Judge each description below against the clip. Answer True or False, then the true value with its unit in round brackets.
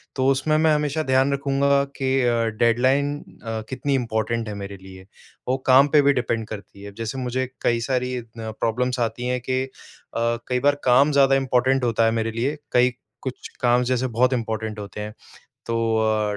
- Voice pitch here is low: True (125 Hz)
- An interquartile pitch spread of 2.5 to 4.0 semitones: True (3.0 semitones)